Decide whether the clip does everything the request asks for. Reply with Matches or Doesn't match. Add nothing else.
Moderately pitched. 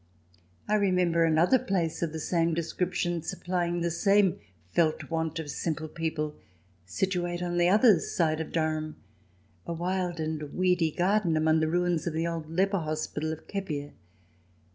Matches